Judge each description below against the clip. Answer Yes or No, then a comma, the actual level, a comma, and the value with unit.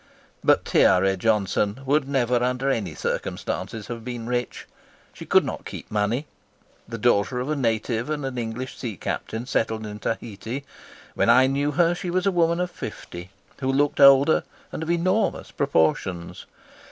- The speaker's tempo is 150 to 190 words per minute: Yes, average, 165 wpm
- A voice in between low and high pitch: No, low, 125 Hz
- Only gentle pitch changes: No, average, 4.2 semitones